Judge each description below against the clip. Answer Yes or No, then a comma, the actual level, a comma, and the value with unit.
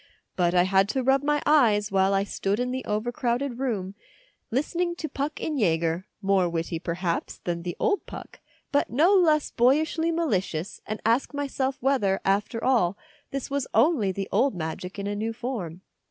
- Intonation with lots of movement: Yes, wide, 6.5 semitones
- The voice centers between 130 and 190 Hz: No, high, 225 Hz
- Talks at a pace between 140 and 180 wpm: Yes, average, 175 wpm